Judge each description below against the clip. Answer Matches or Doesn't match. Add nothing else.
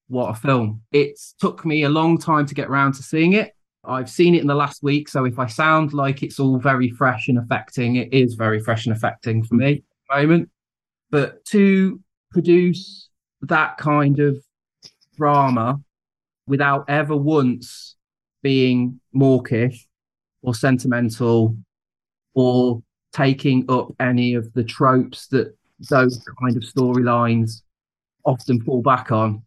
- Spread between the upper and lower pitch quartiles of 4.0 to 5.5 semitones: Doesn't match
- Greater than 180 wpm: Doesn't match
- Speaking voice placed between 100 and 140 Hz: Matches